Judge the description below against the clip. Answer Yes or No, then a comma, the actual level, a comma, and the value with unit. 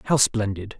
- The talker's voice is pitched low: Yes, low, 110 Hz